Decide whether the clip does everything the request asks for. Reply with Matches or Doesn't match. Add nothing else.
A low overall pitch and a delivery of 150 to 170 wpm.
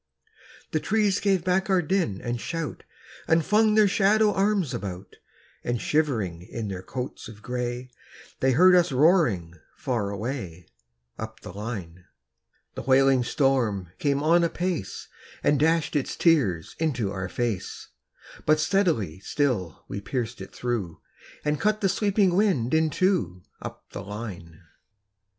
Doesn't match